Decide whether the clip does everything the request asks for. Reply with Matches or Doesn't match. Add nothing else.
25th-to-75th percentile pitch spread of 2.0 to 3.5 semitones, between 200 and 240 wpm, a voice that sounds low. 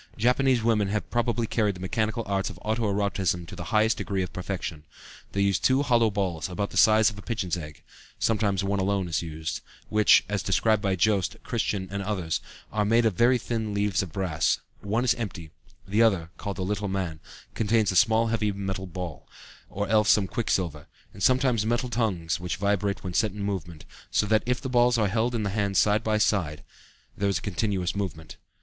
Matches